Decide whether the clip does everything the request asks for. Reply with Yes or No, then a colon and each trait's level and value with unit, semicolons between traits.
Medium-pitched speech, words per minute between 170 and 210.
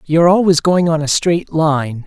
Yes: medium, 160 Hz; fast, 205 wpm